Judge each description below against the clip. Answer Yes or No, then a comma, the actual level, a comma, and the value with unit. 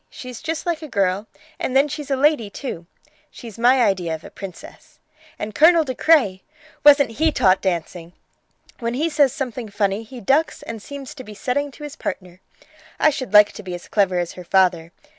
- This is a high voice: Yes, high, 235 Hz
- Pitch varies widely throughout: Yes, wide, 7.1 semitones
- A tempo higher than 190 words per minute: Yes, average, 200 wpm